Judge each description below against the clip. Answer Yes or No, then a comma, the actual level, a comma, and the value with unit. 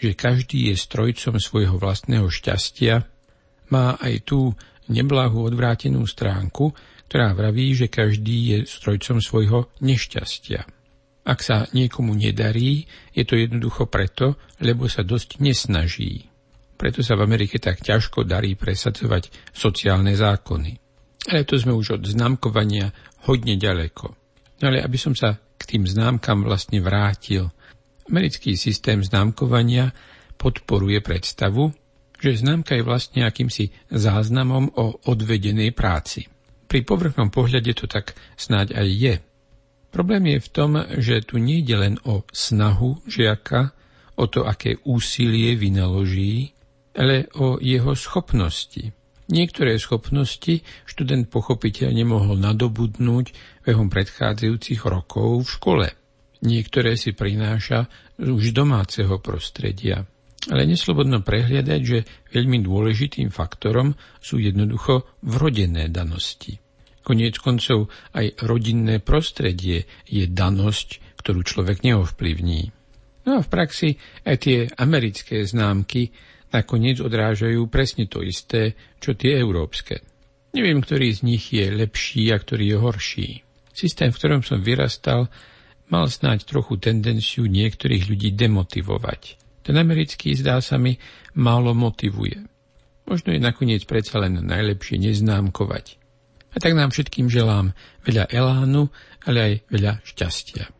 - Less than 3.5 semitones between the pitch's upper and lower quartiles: No, average, 3.8 semitones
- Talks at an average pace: Yes, average, 120 wpm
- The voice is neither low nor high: No, low, 115 Hz